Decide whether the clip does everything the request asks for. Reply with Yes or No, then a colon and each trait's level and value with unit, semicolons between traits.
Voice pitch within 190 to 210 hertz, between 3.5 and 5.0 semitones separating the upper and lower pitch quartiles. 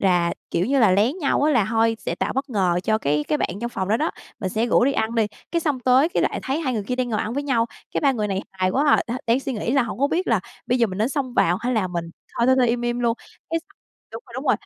No: high, 235 Hz; average, 4.3 semitones